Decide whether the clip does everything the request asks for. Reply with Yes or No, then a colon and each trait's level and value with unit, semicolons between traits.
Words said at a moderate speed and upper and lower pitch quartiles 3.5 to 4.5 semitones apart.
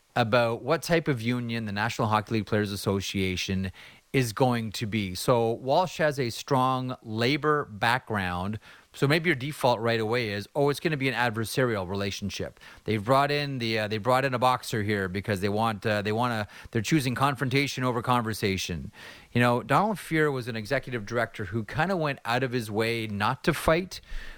Yes: average, 195 wpm; average, 4.1 semitones